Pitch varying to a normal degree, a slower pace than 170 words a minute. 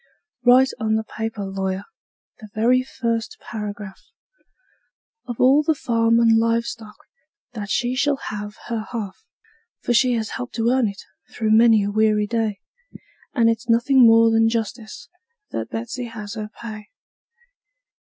No: narrow, 2.1 semitones; average, 150 wpm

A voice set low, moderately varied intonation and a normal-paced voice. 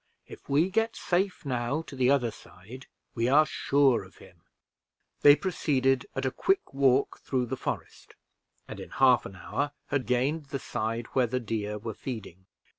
Yes: low, 130 Hz; average, 3.4 semitones; average, 175 wpm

